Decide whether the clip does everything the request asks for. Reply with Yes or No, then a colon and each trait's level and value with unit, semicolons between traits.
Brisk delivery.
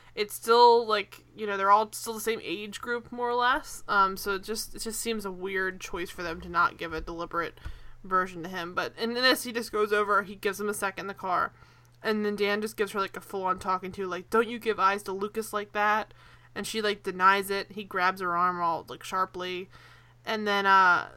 Yes: fast, 245 wpm